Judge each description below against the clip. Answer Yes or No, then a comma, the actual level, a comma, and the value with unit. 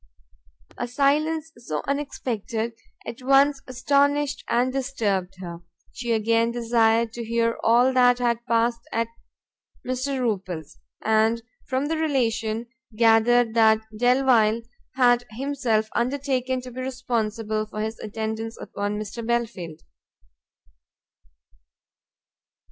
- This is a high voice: Yes, high, 235 Hz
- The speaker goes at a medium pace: No, slow, 110 wpm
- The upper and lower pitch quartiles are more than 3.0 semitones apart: No, average, 2.7 semitones